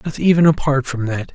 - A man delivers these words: Yes, male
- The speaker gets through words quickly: Yes, fast, 225 wpm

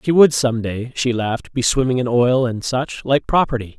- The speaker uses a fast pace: Yes, fast, 220 wpm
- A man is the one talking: Yes, male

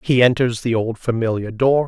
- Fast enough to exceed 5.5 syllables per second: No, 5.0 syllables/s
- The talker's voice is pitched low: Yes, low, 120 Hz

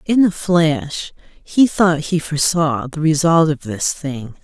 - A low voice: No, medium, 160 Hz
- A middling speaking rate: Yes, average, 160 wpm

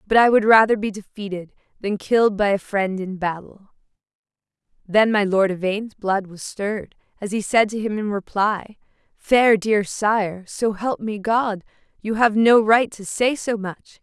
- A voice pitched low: No, high, 210 Hz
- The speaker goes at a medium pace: Yes, average, 180 wpm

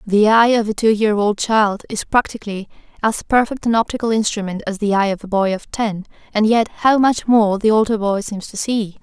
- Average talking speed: No, fast, 225 wpm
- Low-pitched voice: No, high, 215 Hz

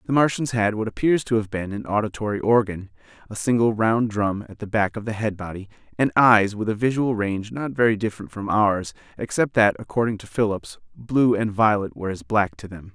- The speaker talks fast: Yes, fast, 215 wpm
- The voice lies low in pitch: Yes, low, 105 Hz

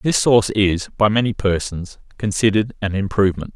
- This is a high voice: No, low, 105 Hz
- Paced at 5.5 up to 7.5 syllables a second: Yes, 5.6 syllables/s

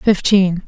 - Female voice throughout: Yes, female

